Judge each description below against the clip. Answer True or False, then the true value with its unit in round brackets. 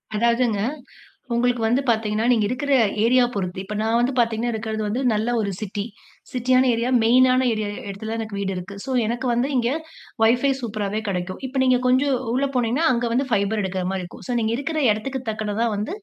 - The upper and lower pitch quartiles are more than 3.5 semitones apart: False (3.2 semitones)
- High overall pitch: True (230 Hz)